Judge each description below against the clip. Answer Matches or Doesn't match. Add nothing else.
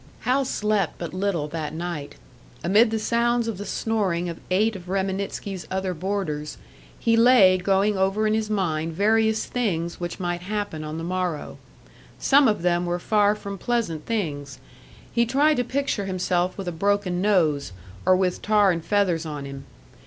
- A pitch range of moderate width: Matches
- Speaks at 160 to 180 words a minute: Matches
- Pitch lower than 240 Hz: Matches